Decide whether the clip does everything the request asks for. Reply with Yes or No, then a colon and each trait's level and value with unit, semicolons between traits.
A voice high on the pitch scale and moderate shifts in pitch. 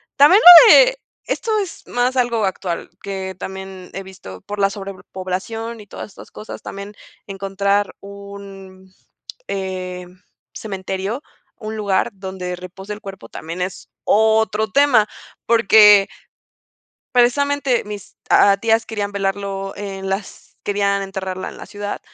No: high, 200 Hz; narrow, 2.3 semitones